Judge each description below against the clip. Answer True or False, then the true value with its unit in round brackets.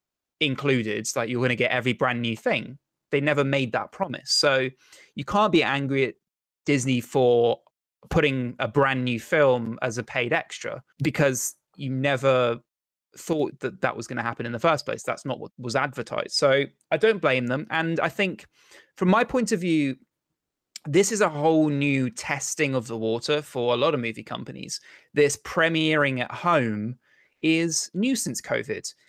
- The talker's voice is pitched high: False (135 Hz)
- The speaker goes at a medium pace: True (180 wpm)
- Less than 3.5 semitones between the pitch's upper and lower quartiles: False (4.1 semitones)